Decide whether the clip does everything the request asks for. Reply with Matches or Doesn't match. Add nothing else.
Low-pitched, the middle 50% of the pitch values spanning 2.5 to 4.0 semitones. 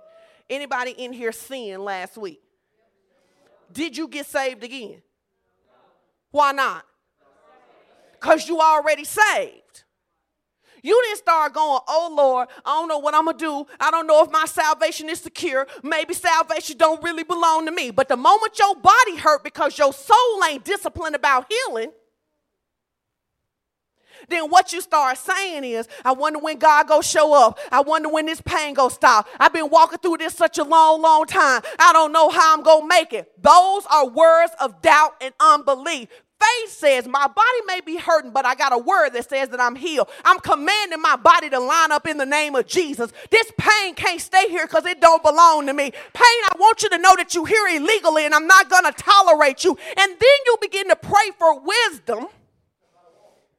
Doesn't match